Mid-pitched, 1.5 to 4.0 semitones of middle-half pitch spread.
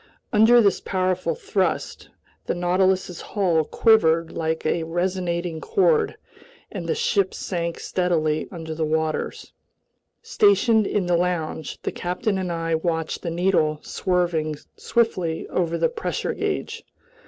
Yes: medium, 180 Hz; average, 3.4 semitones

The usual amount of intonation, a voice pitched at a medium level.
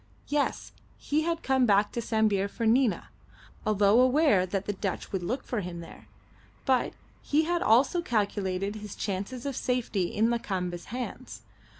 No: average, 4.6 semitones; high, 220 Hz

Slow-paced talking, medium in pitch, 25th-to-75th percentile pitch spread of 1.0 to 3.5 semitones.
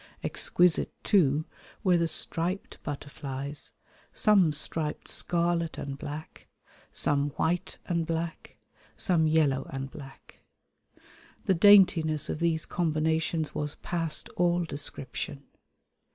Yes: slow, 105 wpm; medium, 160 Hz; average, 2.8 semitones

